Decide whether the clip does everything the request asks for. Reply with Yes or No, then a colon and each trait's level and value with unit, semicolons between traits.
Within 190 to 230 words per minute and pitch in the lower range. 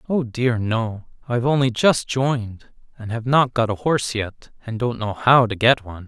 Yes: fast, 205 wpm; low, 120 Hz